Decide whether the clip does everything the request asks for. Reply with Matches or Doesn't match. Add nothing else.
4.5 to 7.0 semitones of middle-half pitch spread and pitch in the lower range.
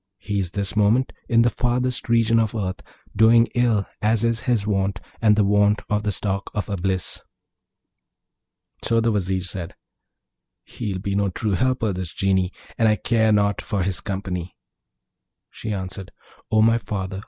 Doesn't match